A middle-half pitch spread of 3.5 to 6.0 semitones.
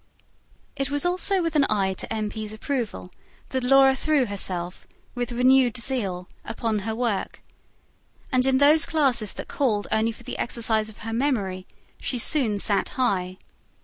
Yes: average, 4.3 semitones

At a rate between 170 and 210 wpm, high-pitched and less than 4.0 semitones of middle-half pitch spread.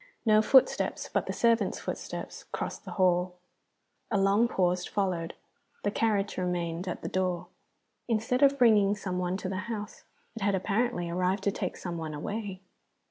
No: average, 160 wpm; high, 195 Hz; average, 3.1 semitones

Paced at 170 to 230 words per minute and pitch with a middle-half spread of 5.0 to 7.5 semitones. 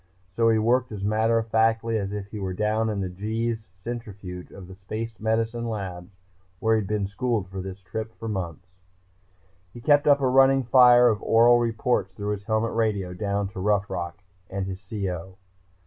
No: average, 195 wpm; average, 3.0 semitones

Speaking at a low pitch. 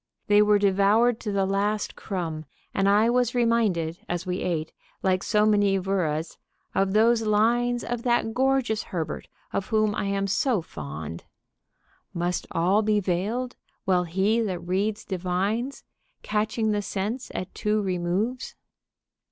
No: high, 205 Hz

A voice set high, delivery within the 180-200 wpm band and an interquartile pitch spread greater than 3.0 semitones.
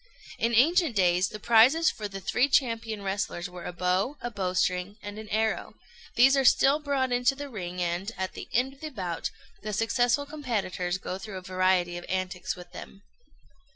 Yes: high, 210 Hz; average, 190 wpm; average, 5.3 semitones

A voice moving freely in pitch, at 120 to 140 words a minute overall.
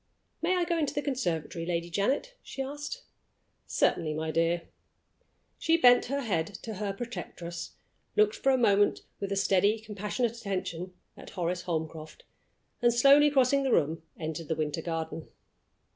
No: wide, 8.2 semitones; average, 155 wpm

